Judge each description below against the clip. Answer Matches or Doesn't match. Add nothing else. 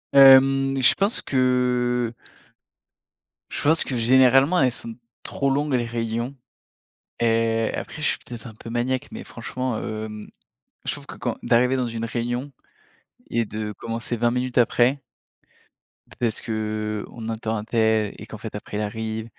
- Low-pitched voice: Matches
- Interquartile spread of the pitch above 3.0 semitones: Doesn't match